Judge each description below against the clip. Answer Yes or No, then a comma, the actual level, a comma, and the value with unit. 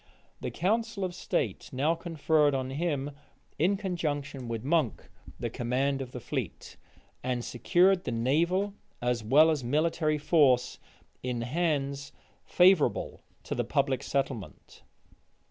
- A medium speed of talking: No, slow, 130 wpm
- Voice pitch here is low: No, medium, 145 Hz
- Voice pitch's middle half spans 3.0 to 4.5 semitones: No, average, 5.0 semitones